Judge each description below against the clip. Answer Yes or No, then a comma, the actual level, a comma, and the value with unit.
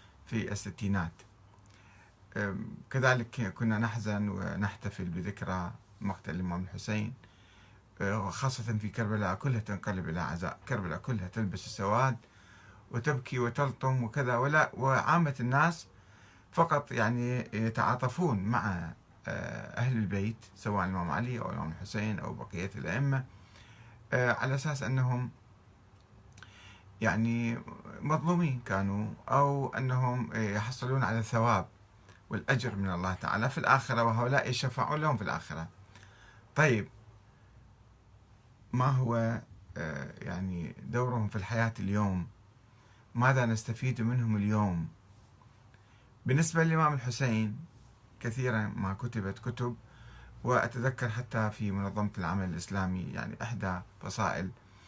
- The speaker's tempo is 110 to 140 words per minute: No, average, 100 wpm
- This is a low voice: Yes, low, 110 Hz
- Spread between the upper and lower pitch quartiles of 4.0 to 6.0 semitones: No, average, 3.6 semitones